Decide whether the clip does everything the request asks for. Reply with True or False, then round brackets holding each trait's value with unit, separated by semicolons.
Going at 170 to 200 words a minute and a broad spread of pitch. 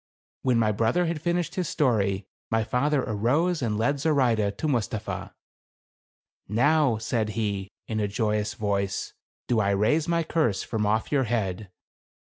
False (155 wpm; 5.7 semitones)